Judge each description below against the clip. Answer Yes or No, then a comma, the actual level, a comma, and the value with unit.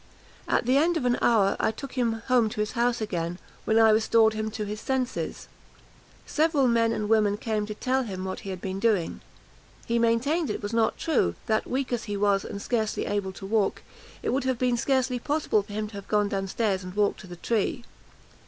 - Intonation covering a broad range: No, average, 3.2 semitones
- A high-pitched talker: Yes, high, 220 Hz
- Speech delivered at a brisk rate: Yes, fast, 220 wpm